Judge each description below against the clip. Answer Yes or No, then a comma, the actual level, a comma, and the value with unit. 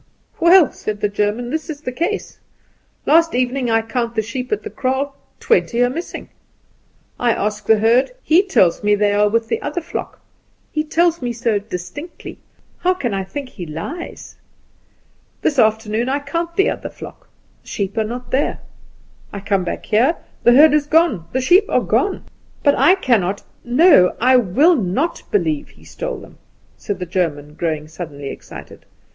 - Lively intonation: Yes, wide, 7.1 semitones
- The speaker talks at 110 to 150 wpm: No, average, 175 wpm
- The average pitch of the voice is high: Yes, high, 245 Hz